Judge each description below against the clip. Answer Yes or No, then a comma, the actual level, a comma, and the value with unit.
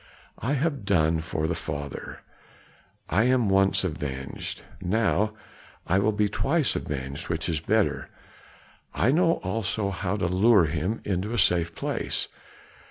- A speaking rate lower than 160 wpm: Yes, average, 140 wpm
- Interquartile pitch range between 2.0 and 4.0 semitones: No, average, 5.0 semitones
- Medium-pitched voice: No, very low, 95 Hz